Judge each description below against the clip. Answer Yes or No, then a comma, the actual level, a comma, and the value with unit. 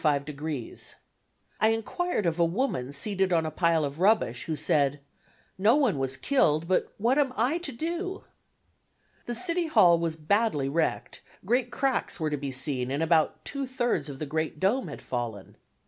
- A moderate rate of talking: Yes, average, 170 wpm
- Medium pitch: Yes, medium, 170 Hz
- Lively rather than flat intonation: Yes, wide, 8.6 semitones